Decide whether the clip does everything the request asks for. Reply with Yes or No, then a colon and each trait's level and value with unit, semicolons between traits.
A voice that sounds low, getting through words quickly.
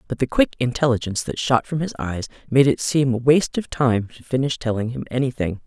Yes: low, 130 Hz; fast, 210 wpm